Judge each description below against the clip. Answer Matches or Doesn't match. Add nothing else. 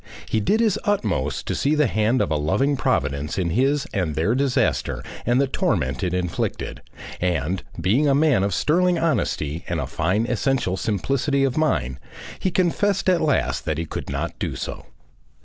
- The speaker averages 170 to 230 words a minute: Matches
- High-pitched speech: Doesn't match